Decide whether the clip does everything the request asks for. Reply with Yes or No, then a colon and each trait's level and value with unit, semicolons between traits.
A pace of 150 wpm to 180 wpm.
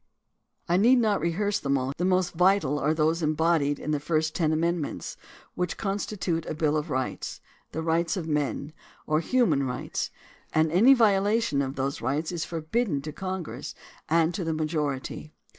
Yes: average, 175 wpm